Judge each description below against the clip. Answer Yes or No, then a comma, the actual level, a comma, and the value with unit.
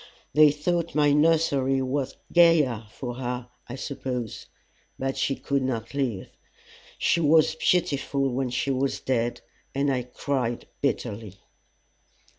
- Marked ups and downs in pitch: No, average, 3.0 semitones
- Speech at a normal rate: No, slow, 125 wpm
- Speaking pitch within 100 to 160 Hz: Yes, low, 135 Hz